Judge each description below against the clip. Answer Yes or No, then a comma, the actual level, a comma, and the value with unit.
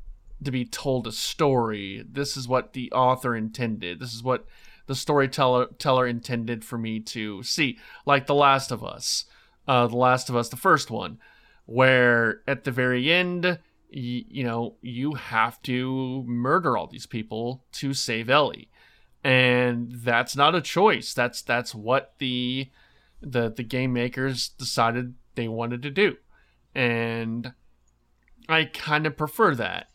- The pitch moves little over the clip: Yes, narrow, 2.1 semitones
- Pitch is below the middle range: Yes, low, 125 Hz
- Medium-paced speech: Yes, average, 150 wpm